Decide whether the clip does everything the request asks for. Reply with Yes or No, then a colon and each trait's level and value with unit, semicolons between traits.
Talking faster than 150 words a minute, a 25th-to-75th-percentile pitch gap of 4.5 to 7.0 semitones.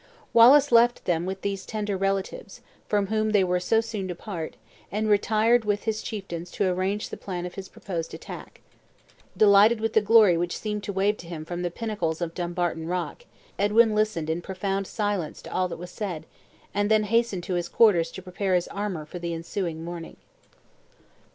No: average, 190 wpm; average, 3.5 semitones